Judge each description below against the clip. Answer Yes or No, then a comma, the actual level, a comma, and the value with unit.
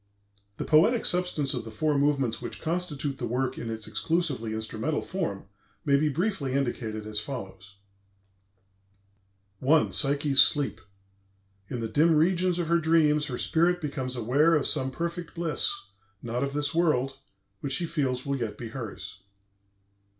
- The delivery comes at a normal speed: Yes, average, 150 wpm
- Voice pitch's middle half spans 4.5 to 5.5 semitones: Yes, average, 5.1 semitones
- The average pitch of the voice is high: No, medium, 140 Hz